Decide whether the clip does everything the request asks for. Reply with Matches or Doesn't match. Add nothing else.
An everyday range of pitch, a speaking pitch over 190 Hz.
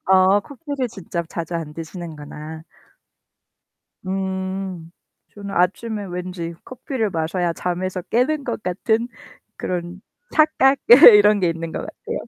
Doesn't match